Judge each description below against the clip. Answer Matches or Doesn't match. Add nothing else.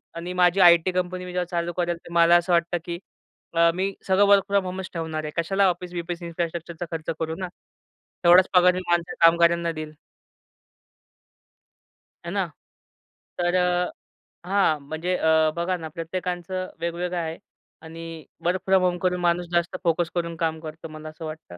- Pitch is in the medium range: Matches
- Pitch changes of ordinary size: Doesn't match